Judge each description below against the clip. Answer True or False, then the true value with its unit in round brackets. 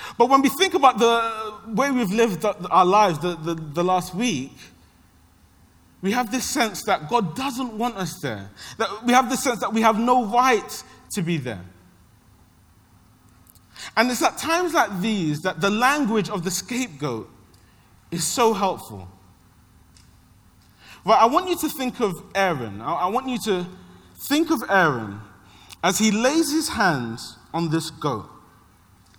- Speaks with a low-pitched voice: False (185 Hz)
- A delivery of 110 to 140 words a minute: False (160 wpm)